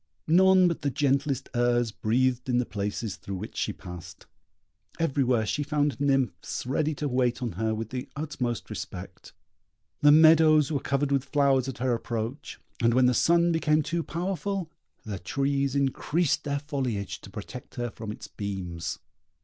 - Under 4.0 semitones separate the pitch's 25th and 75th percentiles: No, average, 4.3 semitones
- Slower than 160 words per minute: No, average, 165 wpm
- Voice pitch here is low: Yes, low, 130 Hz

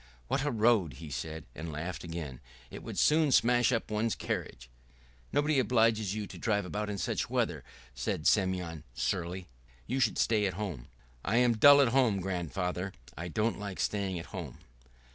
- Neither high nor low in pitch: No, low, 100 Hz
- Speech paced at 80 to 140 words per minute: No, average, 175 wpm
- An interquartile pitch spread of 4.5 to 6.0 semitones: Yes, average, 5.2 semitones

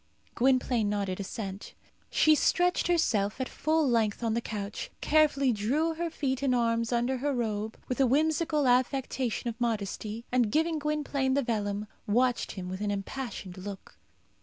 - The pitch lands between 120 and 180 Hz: No, high, 245 Hz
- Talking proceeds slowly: No, average, 160 wpm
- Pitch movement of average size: Yes, average, 4.9 semitones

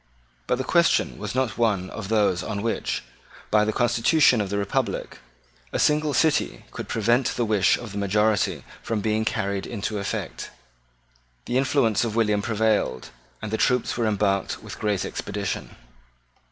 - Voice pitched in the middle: No, low, 110 Hz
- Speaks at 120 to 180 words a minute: Yes, average, 160 wpm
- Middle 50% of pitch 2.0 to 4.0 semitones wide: Yes, average, 2.7 semitones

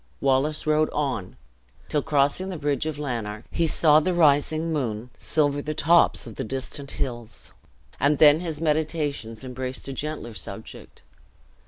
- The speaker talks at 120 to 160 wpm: Yes, average, 150 wpm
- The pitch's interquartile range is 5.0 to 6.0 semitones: No, average, 3.1 semitones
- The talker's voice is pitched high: No, medium, 145 Hz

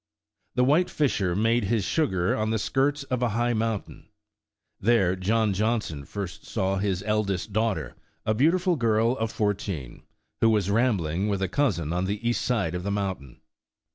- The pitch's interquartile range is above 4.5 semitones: No, average, 3.8 semitones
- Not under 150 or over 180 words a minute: Yes, average, 170 wpm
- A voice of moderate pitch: No, low, 105 Hz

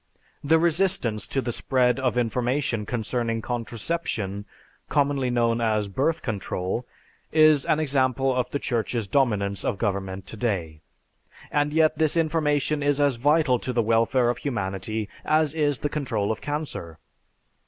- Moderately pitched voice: No, low, 125 Hz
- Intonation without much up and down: No, average, 4.8 semitones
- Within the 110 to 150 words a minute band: Yes, average, 145 wpm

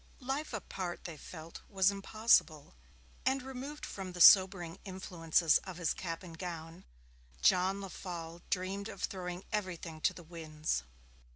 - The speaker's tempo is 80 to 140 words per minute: Yes, slow, 135 wpm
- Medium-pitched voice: Yes, medium, 180 Hz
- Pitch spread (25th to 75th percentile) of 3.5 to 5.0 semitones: No, average, 2.9 semitones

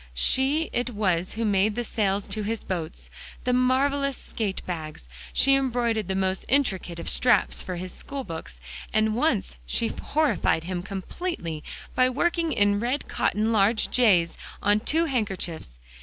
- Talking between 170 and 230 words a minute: No, average, 155 wpm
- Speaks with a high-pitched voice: Yes, high, 215 Hz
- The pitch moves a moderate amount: No, wide, 5.7 semitones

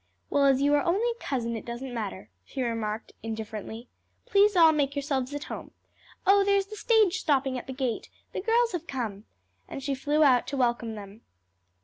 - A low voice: No, very high, 270 Hz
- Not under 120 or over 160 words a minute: No, average, 195 wpm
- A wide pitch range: Yes, wide, 6.6 semitones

